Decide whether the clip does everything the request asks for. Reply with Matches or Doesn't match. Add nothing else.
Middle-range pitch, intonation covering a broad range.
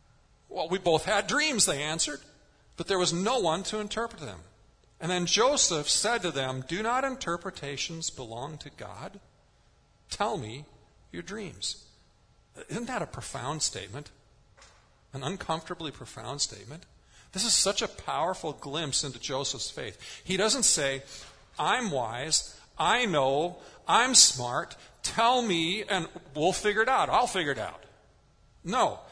Matches